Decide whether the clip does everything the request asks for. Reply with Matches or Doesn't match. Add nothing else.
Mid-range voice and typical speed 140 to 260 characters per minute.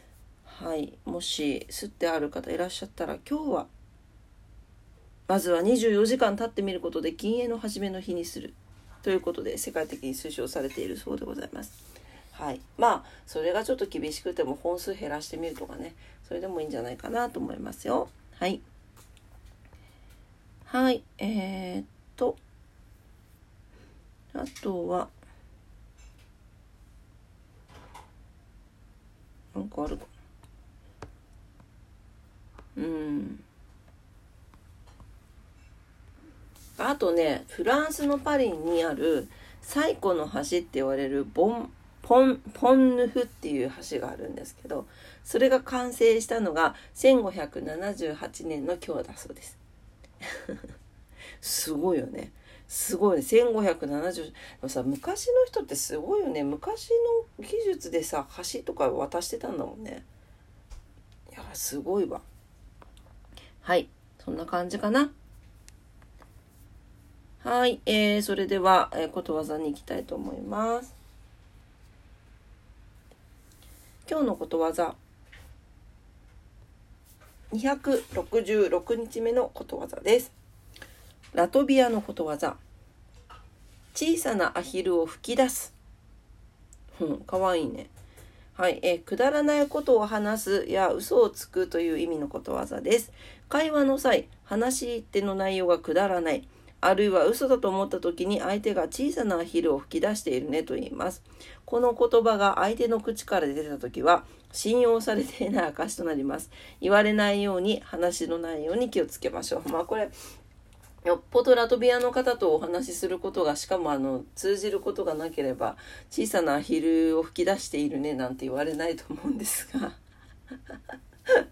Matches